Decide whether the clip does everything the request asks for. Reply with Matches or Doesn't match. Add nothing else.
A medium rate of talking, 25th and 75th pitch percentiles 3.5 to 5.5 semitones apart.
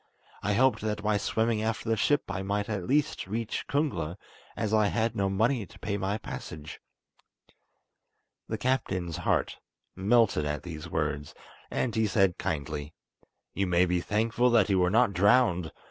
Matches